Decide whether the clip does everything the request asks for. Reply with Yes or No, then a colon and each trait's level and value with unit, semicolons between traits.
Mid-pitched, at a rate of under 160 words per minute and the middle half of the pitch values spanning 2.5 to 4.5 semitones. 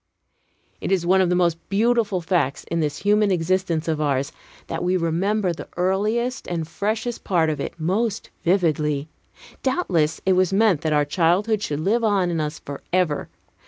No: medium, 180 Hz; average, 170 wpm; average, 4.2 semitones